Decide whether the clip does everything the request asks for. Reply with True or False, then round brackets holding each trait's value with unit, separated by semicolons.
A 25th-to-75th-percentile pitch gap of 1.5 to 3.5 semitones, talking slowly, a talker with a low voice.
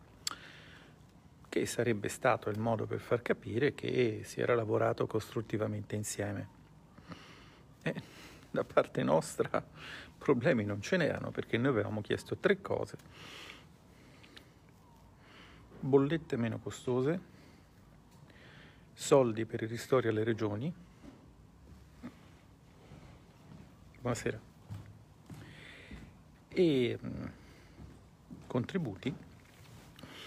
True (2.6 semitones; 85 wpm; 115 Hz)